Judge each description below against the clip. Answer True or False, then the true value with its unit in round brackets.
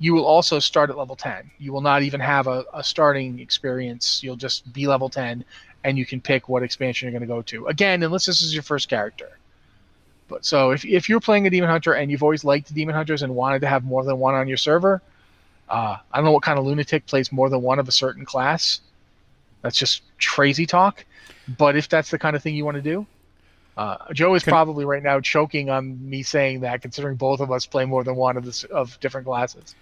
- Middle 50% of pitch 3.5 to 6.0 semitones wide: False (3.0 semitones)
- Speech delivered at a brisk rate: True (240 wpm)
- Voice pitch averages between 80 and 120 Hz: False (140 Hz)